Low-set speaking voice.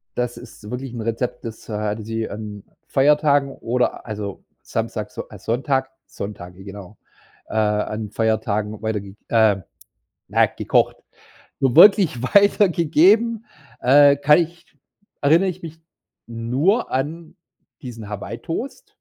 Yes: low, 125 Hz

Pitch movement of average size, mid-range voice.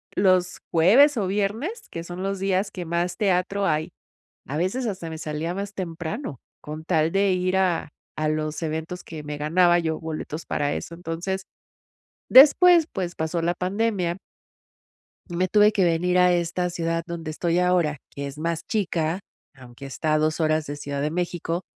Yes: average, 3.1 semitones; medium, 175 Hz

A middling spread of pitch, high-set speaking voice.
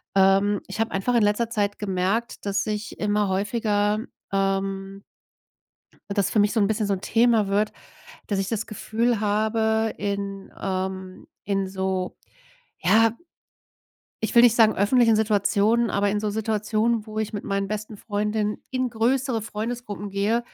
No: narrow, 2.0 semitones; high, 210 Hz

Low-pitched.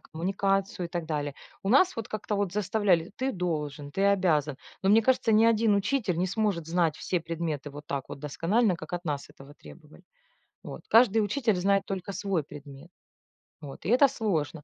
No: medium, 185 Hz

